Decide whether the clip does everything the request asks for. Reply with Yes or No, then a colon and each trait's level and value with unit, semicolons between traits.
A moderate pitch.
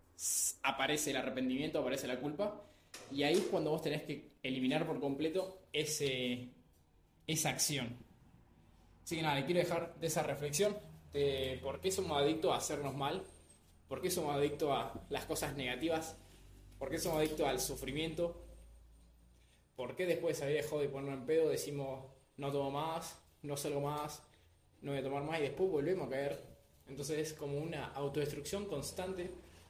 Yes: medium, 145 Hz